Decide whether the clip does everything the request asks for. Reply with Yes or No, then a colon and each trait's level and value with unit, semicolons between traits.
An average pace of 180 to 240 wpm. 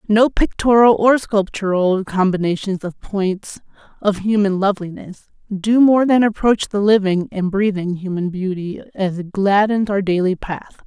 No: average, 145 wpm